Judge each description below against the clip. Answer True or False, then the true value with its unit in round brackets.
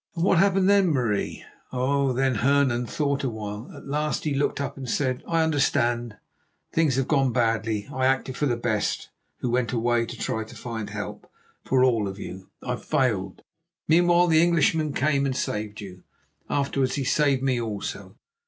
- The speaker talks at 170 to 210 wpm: True (180 wpm)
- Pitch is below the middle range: True (130 Hz)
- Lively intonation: False (3.9 semitones)